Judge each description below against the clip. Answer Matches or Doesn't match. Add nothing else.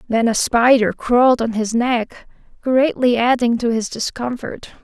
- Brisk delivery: Doesn't match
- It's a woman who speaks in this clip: Matches